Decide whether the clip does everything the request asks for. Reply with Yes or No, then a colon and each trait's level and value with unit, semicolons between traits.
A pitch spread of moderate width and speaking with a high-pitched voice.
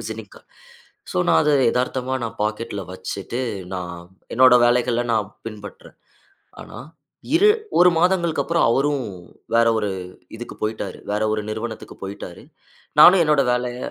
No: average, 3.7 semitones; low, 115 Hz